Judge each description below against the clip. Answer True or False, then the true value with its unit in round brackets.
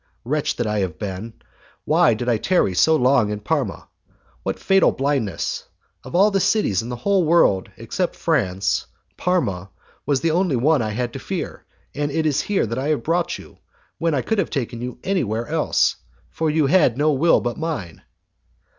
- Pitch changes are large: True (6.6 semitones)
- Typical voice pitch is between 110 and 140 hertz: True (135 Hz)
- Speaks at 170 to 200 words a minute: True (190 wpm)